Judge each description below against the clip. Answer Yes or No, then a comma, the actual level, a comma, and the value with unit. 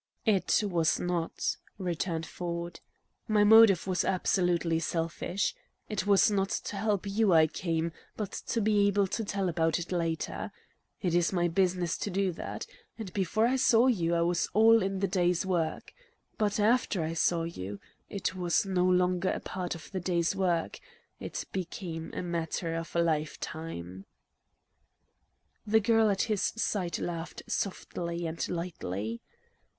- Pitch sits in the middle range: Yes, medium, 180 Hz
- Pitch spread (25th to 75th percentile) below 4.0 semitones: Yes, average, 3.1 semitones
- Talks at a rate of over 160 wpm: No, average, 155 wpm